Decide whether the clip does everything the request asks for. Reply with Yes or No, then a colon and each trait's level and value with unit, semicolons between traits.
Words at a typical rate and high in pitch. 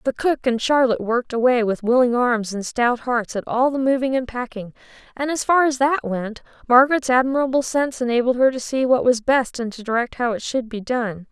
No: fast, 225 wpm; high, 245 Hz